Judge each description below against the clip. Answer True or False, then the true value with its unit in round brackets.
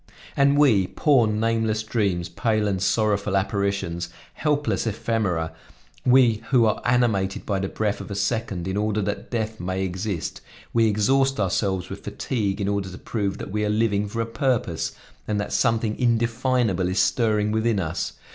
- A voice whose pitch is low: True (105 Hz)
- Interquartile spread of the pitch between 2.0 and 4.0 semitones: True (2.8 semitones)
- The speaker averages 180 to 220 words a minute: False (165 wpm)